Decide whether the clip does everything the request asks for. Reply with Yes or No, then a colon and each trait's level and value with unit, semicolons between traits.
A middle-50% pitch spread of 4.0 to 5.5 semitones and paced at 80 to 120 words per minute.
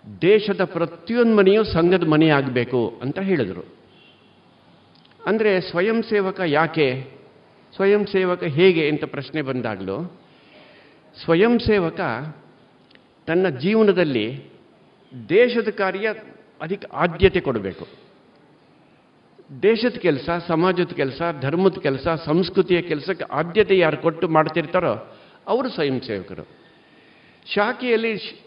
Yes: average, 4.5 semitones; average, 90 wpm